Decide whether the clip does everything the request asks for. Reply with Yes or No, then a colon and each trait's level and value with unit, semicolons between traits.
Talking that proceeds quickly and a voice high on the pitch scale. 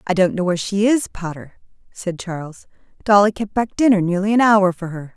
Yes: fast, 210 wpm; high, 195 Hz